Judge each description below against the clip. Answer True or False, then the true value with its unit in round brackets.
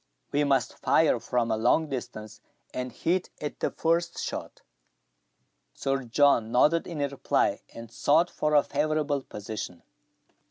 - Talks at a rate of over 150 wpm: False (135 wpm)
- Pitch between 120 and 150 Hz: True (140 Hz)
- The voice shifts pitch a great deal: False (4.4 semitones)